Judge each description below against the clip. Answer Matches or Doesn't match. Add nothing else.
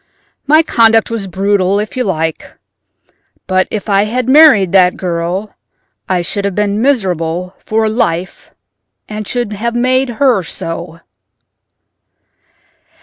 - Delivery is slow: Matches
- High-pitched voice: Matches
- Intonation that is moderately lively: Matches